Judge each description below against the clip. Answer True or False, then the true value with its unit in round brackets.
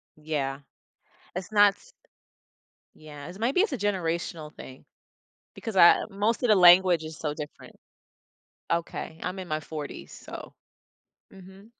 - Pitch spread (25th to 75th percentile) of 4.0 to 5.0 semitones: True (4.6 semitones)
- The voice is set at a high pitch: False (175 Hz)